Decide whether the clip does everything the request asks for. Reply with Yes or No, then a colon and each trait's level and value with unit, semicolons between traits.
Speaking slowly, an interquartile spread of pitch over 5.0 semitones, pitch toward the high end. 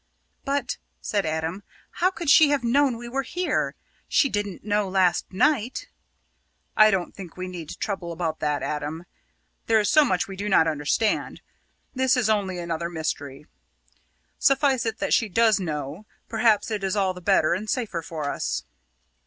No: average, 170 wpm; wide, 5.6 semitones; high, 200 Hz